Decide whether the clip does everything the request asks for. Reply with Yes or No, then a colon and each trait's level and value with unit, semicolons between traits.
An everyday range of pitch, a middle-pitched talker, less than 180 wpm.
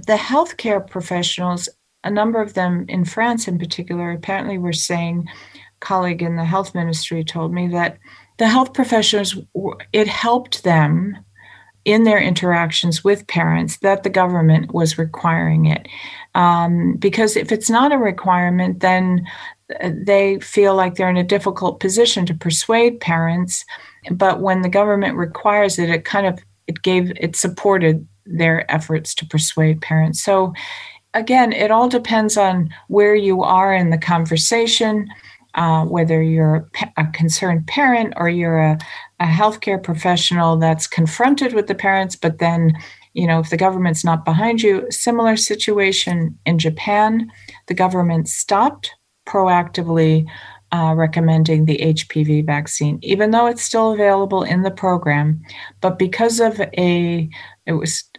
Yes: average, 3.7 semitones; medium, 180 Hz; average, 150 wpm